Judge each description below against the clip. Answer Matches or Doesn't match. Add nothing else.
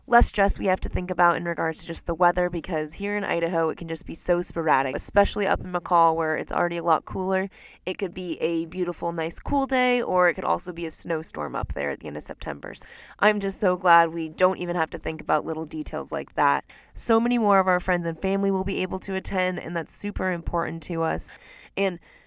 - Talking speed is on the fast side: Matches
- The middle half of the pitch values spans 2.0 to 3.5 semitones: Matches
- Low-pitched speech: Doesn't match